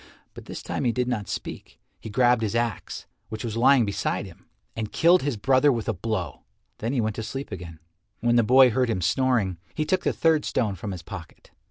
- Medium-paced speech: No, fast, 220 wpm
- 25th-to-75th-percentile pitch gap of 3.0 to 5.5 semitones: Yes, average, 3.6 semitones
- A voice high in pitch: No, low, 115 Hz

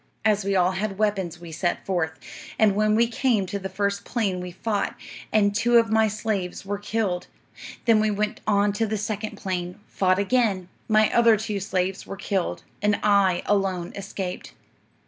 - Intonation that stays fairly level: Yes, narrow, 2.3 semitones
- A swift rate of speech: No, average, 180 wpm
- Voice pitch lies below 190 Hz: No, high, 200 Hz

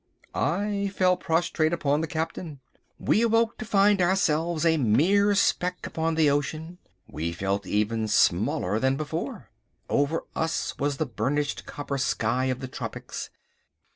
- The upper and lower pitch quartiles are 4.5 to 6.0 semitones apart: Yes, average, 5.1 semitones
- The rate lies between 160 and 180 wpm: No, average, 145 wpm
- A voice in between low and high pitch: Yes, medium, 160 Hz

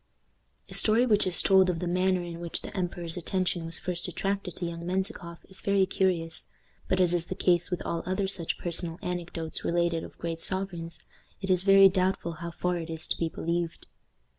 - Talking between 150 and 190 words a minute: No, average, 200 wpm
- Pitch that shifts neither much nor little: No, narrow, 1.9 semitones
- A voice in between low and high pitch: Yes, medium, 175 Hz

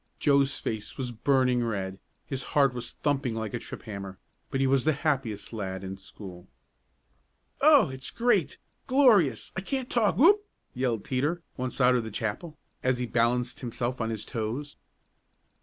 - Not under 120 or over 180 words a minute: Yes, average, 160 wpm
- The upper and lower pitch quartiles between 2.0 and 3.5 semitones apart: No, average, 4.7 semitones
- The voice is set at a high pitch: No, low, 125 Hz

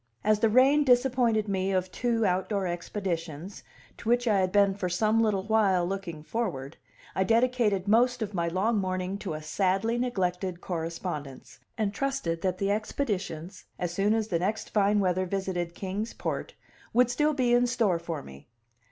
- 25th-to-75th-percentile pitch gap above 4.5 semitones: No, average, 3.9 semitones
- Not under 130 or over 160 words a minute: No, average, 170 wpm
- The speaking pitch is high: Yes, high, 195 Hz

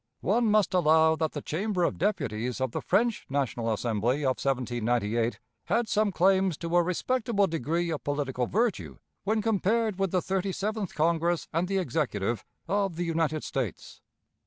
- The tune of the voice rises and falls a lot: Yes, wide, 6.5 semitones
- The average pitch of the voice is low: No, medium, 170 Hz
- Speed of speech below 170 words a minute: Yes, average, 160 wpm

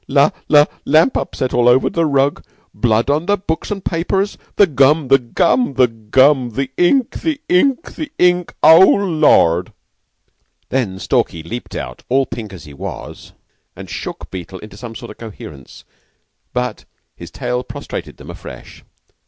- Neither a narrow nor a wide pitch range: No, wide, 6.7 semitones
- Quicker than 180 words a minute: No, average, 160 wpm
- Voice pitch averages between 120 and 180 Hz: Yes, low, 135 Hz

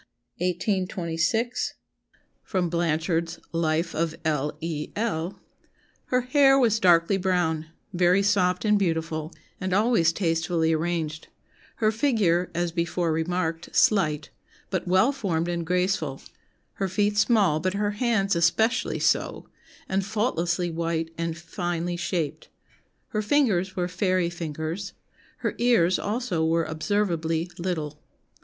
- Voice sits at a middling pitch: Yes, medium, 175 Hz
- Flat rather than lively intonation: No, average, 3.5 semitones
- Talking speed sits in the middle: No, slow, 120 wpm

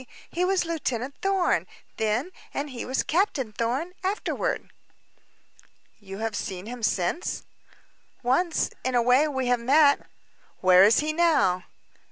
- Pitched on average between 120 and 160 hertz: No, very high, 260 Hz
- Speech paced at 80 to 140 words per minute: Yes, slow, 135 wpm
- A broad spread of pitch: Yes, wide, 6.7 semitones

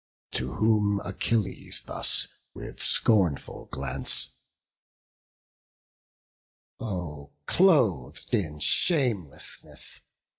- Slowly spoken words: Yes, slow, 65 wpm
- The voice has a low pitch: Yes, very low, 95 Hz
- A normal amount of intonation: No, wide, 7.8 semitones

